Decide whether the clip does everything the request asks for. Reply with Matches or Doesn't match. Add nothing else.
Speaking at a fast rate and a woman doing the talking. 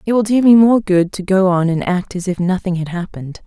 Matches